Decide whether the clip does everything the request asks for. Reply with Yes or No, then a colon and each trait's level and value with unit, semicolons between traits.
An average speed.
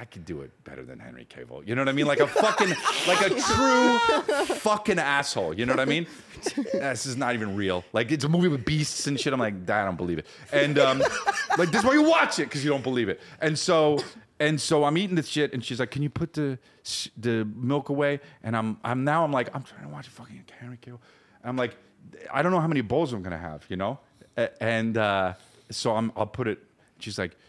No: fast, 250 wpm